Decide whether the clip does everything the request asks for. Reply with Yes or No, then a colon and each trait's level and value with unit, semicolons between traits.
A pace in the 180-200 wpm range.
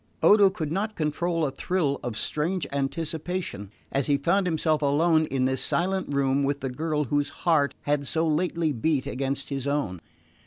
No: average, 170 wpm